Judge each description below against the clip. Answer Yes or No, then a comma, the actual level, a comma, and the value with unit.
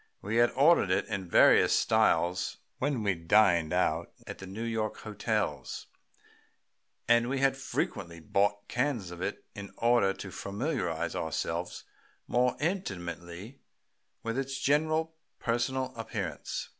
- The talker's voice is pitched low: Yes, low, 115 Hz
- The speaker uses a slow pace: Yes, slow, 130 wpm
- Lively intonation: Yes, wide, 5.7 semitones